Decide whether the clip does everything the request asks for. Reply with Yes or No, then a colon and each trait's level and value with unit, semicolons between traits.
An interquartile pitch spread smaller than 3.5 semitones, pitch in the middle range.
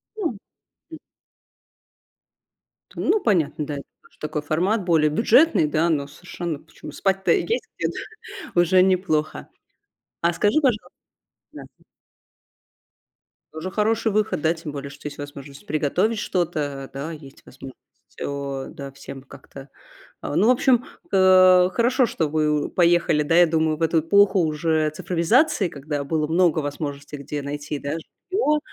No: average, 4.6 semitones; medium, 160 Hz